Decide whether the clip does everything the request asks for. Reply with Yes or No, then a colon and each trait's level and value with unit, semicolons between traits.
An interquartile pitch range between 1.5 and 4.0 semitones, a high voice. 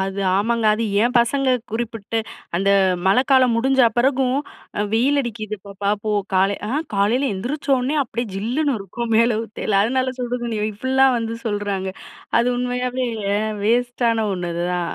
Yes: average, 3.7 semitones; high, 235 Hz